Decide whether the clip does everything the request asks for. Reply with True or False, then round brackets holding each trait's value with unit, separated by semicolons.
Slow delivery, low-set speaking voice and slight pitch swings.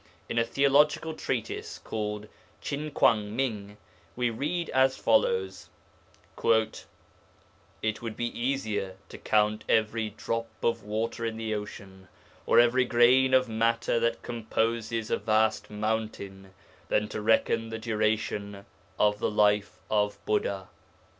True (125 wpm; 110 Hz; 2.1 semitones)